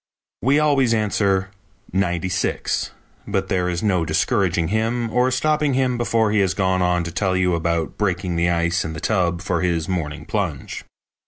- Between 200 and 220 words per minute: No, average, 175 wpm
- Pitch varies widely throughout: No, average, 4.3 semitones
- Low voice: Yes, very low, 95 Hz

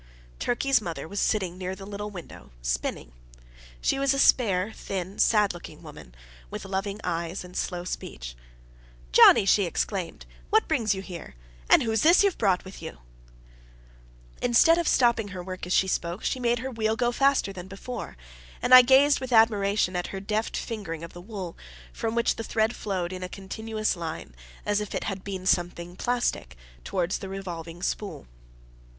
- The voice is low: No, high, 195 Hz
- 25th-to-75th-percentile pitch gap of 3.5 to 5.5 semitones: Yes, average, 4.1 semitones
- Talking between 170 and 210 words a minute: Yes, average, 175 wpm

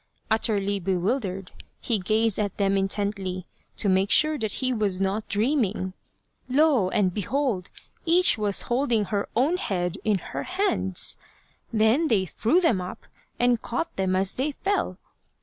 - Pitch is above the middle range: Yes, high, 210 Hz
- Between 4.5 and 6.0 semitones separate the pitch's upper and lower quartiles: Yes, average, 5.0 semitones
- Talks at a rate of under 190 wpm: Yes, average, 150 wpm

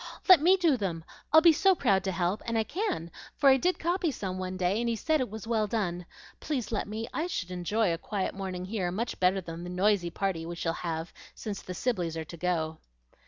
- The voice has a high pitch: Yes, high, 195 Hz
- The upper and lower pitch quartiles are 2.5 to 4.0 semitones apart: No, average, 5.2 semitones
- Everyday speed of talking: No, fast, 235 wpm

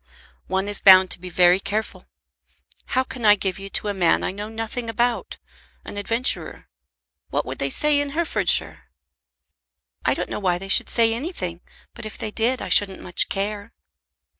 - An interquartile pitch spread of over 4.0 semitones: No, average, 3.6 semitones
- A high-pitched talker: Yes, high, 205 Hz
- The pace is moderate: Yes, average, 180 wpm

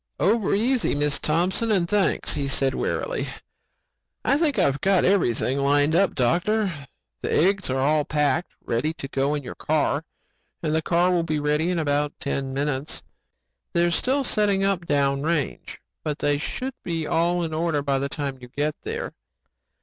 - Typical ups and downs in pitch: Yes, average, 4.3 semitones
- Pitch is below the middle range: No, medium, 155 Hz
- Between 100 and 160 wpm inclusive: No, average, 175 wpm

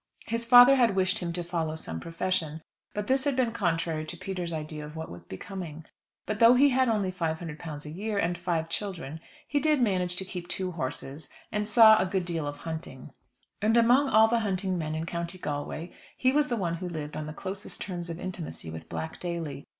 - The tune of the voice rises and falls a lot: No, average, 4.9 semitones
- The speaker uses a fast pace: Yes, fast, 210 wpm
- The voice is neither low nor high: Yes, medium, 175 Hz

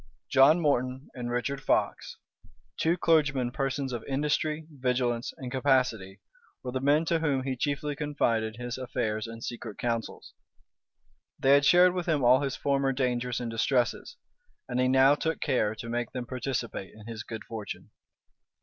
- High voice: No, low, 130 Hz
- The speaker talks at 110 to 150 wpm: No, average, 160 wpm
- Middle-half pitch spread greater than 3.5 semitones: No, average, 2.9 semitones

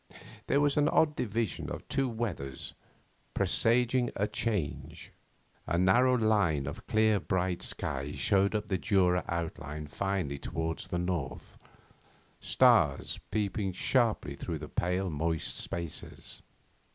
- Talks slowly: Yes, slow, 125 wpm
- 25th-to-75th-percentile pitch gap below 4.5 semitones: No, wide, 5.5 semitones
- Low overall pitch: Yes, very low, 95 Hz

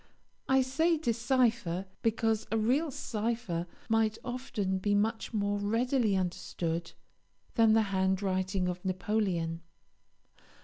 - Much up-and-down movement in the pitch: No, average, 3.8 semitones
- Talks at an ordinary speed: No, slow, 105 wpm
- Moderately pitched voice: No, high, 215 Hz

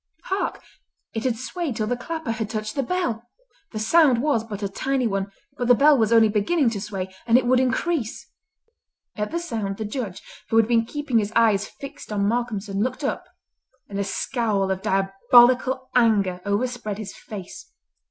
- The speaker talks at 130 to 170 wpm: No, average, 180 wpm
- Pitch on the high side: Yes, high, 230 Hz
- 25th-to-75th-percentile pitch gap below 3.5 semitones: No, average, 3.8 semitones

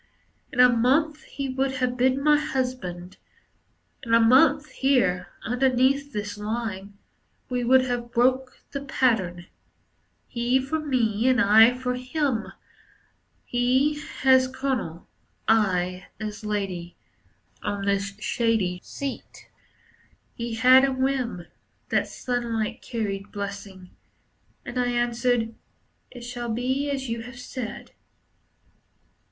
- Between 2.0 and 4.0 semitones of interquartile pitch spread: Yes, average, 3.5 semitones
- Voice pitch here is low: No, high, 245 Hz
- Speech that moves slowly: Yes, slow, 115 wpm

